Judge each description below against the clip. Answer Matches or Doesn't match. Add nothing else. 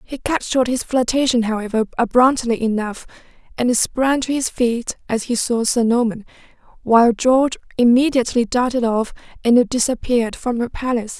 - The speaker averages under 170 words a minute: Matches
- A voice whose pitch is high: Matches